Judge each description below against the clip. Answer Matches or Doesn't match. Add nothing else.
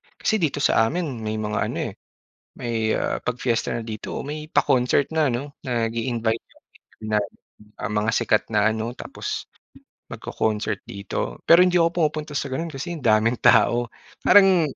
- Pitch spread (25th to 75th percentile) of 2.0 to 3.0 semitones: Doesn't match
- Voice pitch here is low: Matches